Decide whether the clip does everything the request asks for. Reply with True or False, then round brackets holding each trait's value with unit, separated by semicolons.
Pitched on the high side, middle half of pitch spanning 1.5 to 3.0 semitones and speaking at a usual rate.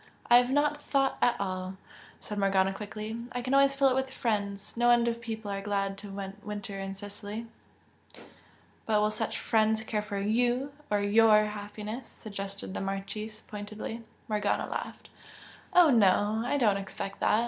True (215 Hz; 2.7 semitones; 170 wpm)